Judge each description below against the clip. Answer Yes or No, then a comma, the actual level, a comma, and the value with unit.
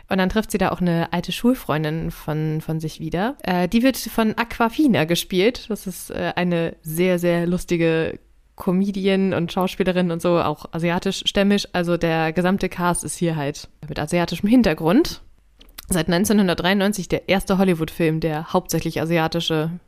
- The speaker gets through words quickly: No, average, 155 wpm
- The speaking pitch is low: No, medium, 175 Hz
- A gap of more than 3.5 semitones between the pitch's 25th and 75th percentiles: No, average, 2.9 semitones